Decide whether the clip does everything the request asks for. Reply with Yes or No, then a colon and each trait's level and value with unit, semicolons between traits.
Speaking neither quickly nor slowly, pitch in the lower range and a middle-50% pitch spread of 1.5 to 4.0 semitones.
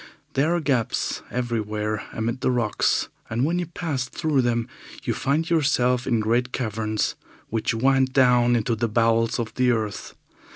Yes: average, 160 wpm; low, 120 Hz; average, 2.9 semitones